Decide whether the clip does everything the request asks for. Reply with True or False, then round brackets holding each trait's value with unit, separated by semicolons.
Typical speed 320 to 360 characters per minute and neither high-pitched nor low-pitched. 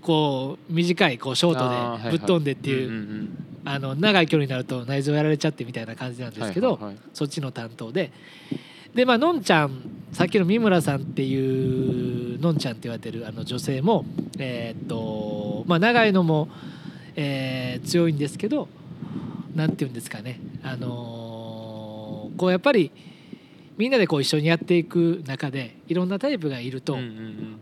True (345 characters per minute; 145 Hz)